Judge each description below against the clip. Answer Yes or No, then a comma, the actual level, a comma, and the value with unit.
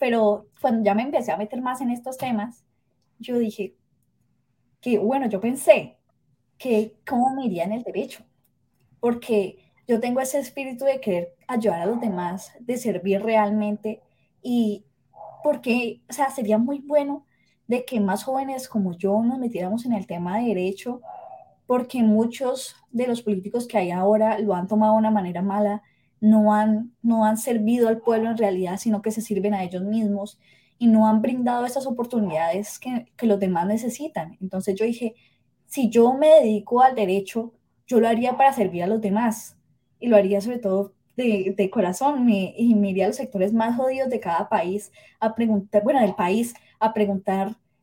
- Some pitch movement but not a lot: Yes, average, 3.2 semitones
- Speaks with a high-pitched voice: Yes, high, 220 Hz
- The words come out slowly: No, average, 180 wpm